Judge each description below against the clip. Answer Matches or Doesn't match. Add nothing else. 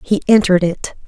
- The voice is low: Doesn't match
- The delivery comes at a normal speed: Matches